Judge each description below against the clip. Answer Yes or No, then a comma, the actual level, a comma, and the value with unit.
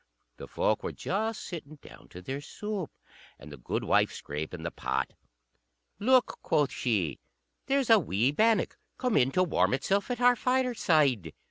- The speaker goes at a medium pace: Yes, average, 155 wpm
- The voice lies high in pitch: No, medium, 160 Hz